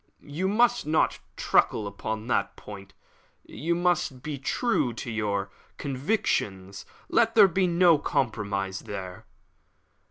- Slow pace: Yes, slow, 120 wpm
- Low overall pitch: Yes, low, 125 Hz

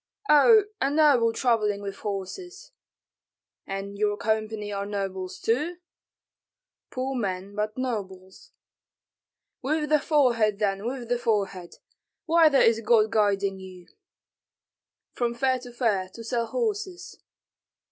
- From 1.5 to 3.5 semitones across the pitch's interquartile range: No, average, 5.1 semitones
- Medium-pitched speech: No, high, 225 Hz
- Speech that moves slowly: Yes, slow, 115 wpm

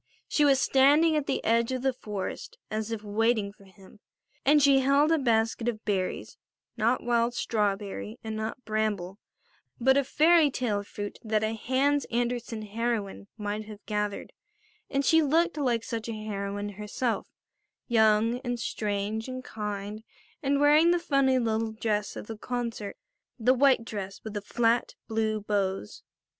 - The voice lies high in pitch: Yes, high, 225 Hz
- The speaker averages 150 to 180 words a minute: Yes, average, 160 wpm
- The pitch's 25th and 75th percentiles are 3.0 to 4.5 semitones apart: Yes, average, 3.7 semitones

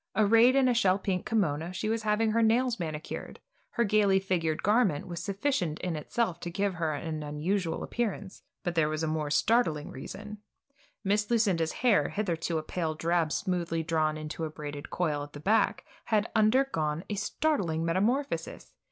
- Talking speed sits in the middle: Yes, average, 170 wpm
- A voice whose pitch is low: No, medium, 180 Hz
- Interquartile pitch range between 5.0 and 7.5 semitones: Yes, average, 5.3 semitones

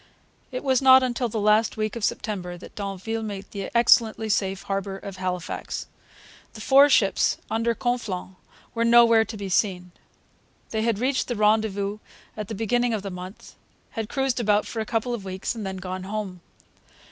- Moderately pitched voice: No, high, 215 Hz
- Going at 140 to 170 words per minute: No, average, 180 wpm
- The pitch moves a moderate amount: Yes, average, 3.1 semitones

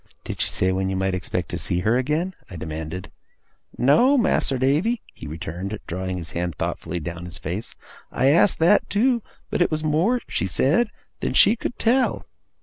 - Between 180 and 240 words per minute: Yes, average, 185 wpm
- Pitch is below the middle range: Yes, low, 115 Hz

